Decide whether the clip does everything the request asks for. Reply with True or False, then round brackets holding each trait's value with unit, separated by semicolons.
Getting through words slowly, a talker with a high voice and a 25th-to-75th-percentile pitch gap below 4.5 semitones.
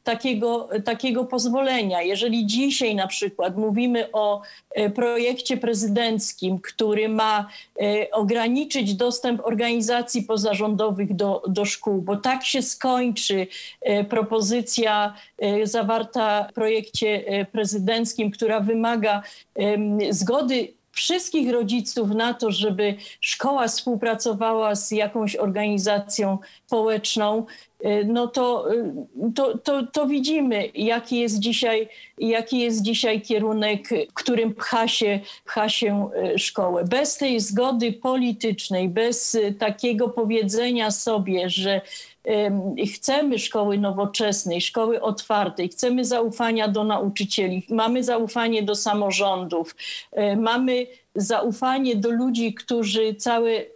True (105 wpm; 225 Hz; 2.4 semitones)